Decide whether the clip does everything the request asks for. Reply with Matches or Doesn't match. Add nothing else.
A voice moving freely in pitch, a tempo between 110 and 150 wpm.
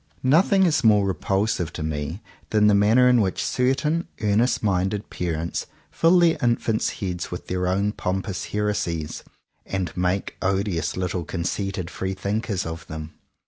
Doesn't match